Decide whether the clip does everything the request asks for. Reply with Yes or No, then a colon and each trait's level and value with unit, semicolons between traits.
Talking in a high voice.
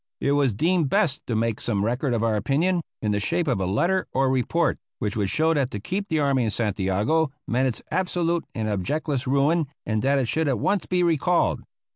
No: low, 135 Hz